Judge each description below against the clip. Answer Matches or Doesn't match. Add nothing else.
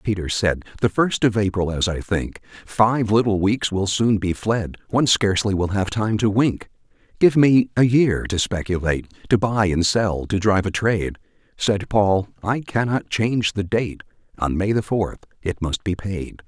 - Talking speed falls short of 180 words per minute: Doesn't match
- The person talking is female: Doesn't match